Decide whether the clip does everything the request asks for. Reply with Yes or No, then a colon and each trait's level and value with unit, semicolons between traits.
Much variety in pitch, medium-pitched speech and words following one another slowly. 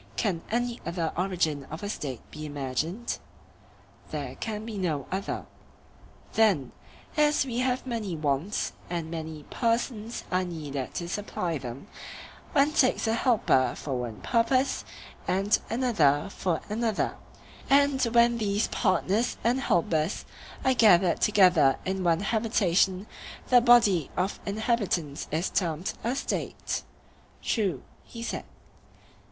No: wide, 6.3 semitones; high, 195 Hz; slow, 125 wpm